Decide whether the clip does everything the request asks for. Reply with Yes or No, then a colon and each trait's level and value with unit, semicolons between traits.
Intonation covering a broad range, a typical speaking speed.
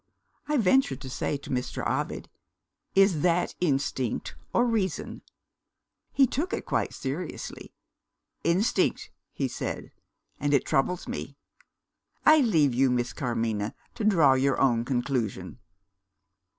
No: wide, 7.4 semitones; slow, 125 wpm